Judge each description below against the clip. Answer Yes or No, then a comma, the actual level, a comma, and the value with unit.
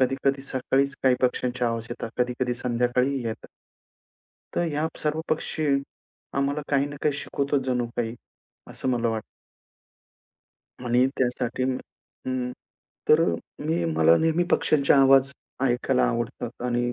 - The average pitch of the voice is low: Yes, low, 130 Hz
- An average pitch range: No, narrow, 2.3 semitones